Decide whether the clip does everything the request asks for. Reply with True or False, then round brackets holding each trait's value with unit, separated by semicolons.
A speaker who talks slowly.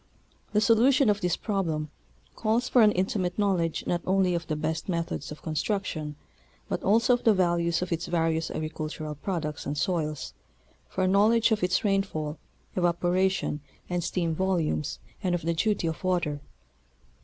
False (160 wpm)